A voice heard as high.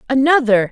Yes: very high, 255 Hz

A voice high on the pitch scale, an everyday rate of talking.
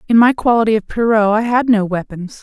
No: high, 220 Hz; fast, 220 wpm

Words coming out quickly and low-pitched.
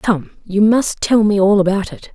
No: fast, 225 wpm; high, 200 Hz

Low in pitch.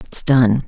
Yes: low, 125 Hz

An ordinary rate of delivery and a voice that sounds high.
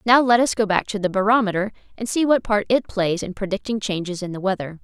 No: fast, 250 wpm; high, 205 Hz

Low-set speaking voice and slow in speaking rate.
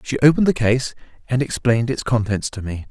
No: low, 125 Hz; fast, 205 wpm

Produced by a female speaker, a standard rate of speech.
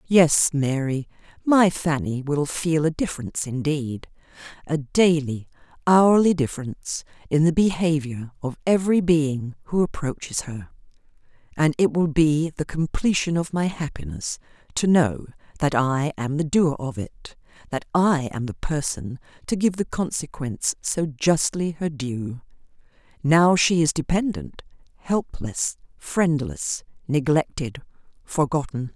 No: female; slow, 125 wpm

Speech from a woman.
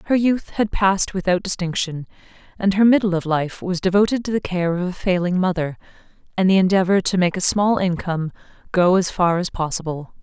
Yes: female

